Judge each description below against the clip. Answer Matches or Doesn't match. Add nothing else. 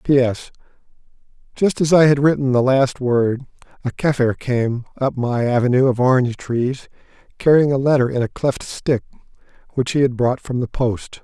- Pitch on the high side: Doesn't match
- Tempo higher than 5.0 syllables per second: Doesn't match